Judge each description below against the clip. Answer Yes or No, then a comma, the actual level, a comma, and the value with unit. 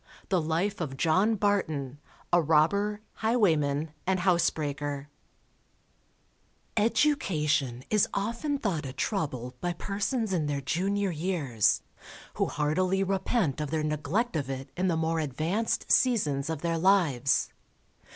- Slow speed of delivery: Yes, slow, 125 wpm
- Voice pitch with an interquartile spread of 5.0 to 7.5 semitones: Yes, average, 5.3 semitones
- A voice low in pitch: No, medium, 165 Hz